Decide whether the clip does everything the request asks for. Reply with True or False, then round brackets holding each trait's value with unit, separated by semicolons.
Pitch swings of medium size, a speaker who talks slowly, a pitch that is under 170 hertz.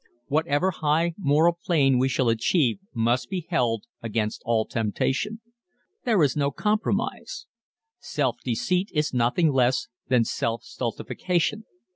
False (6.3 semitones; 125 wpm; 140 Hz)